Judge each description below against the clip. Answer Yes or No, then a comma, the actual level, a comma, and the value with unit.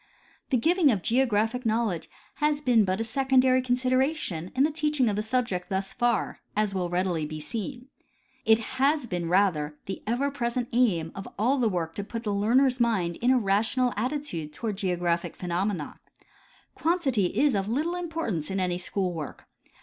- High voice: Yes, high, 225 Hz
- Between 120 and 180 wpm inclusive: Yes, average, 175 wpm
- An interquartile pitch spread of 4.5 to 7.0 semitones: Yes, wide, 5.6 semitones